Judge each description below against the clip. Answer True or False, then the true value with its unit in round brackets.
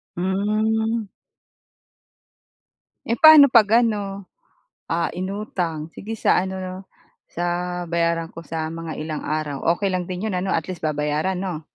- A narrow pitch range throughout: False (3.7 semitones)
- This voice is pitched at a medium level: True (180 Hz)